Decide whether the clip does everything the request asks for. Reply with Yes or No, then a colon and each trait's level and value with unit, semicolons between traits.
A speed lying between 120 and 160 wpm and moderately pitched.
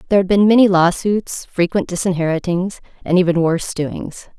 Yes: average, 150 wpm; medium, 180 Hz